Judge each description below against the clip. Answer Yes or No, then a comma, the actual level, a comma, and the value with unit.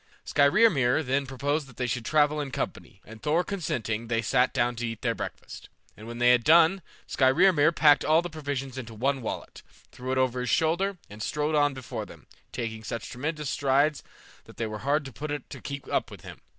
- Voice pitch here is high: No, low, 135 Hz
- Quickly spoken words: Yes, fast, 210 wpm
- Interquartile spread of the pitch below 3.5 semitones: No, average, 3.9 semitones